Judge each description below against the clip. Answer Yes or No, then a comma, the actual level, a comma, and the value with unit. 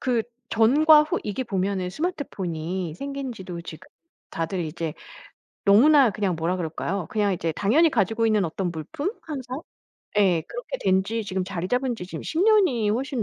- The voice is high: Yes, high, 205 Hz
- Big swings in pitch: Yes, wide, 6.7 semitones